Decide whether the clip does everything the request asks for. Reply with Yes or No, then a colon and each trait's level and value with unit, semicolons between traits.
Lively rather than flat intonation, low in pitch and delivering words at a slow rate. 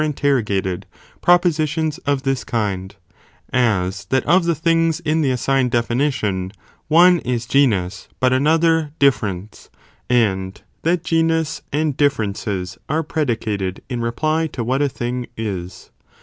Yes: wide, 6.6 semitones; low, 130 Hz; slow, 125 wpm